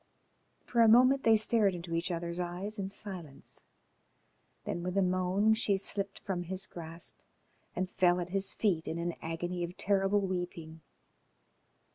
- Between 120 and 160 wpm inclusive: Yes, average, 155 wpm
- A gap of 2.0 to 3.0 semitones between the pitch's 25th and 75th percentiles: Yes, narrow, 2.6 semitones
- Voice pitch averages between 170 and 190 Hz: Yes, medium, 185 Hz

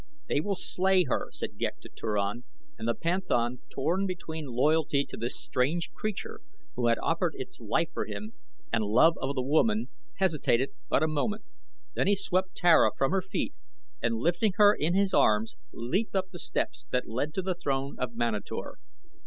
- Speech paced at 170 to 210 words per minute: Yes, average, 180 wpm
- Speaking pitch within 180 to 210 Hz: No, medium, 155 Hz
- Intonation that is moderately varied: No, wide, 7.6 semitones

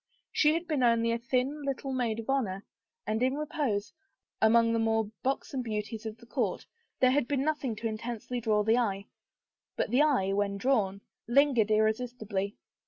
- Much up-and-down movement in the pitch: No, average, 3.5 semitones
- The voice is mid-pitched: No, high, 230 Hz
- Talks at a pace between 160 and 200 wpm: Yes, average, 175 wpm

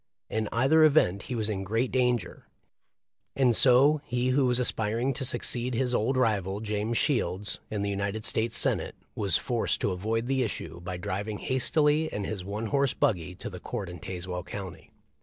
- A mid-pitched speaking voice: No, low, 110 Hz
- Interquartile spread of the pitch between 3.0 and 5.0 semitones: Yes, average, 4.2 semitones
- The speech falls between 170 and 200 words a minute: Yes, average, 185 wpm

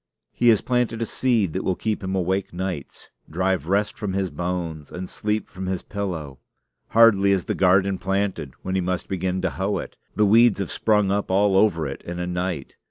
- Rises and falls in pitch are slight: Yes, narrow, 2.3 semitones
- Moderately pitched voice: No, very low, 95 Hz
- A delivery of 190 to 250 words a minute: Yes, fast, 205 wpm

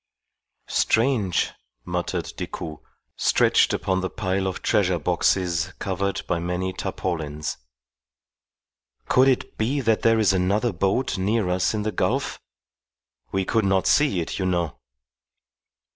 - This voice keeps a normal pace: No, slow, 130 wpm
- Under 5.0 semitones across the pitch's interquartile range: Yes, average, 3.3 semitones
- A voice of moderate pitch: No, very low, 95 Hz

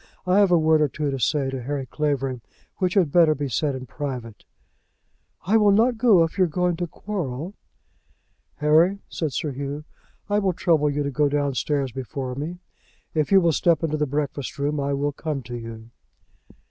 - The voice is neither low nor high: Yes, medium, 150 Hz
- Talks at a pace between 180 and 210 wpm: Yes, average, 195 wpm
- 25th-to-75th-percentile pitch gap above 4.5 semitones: No, average, 4.0 semitones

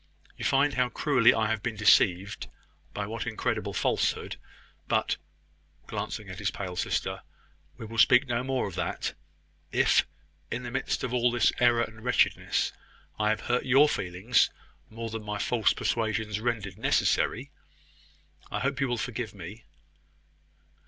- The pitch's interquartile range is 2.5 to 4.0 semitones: Yes, average, 2.8 semitones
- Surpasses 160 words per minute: No, average, 150 wpm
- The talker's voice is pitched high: No, low, 115 Hz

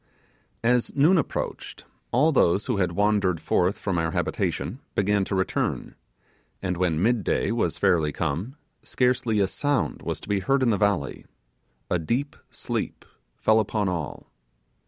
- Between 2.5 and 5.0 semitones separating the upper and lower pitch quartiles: No, wide, 5.4 semitones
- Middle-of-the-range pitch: No, low, 100 Hz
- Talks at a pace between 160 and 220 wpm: No, average, 150 wpm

